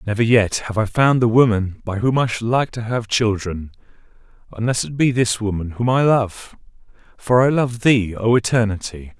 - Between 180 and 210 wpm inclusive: Yes, average, 190 wpm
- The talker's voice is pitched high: No, low, 110 Hz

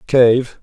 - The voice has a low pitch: Yes, low, 125 Hz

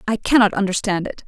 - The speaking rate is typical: Yes, average, 190 wpm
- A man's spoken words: No, female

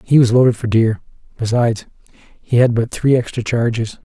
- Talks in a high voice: No, low, 115 Hz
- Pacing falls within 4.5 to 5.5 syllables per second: Yes, 5.3 syllables/s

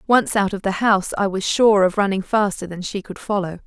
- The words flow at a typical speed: No, fast, 245 wpm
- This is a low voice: No, high, 200 Hz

